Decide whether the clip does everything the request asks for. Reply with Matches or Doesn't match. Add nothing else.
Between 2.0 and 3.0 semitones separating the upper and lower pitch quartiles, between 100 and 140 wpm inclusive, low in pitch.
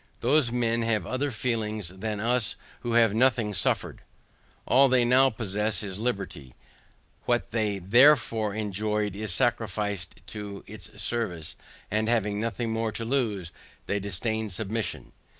Matches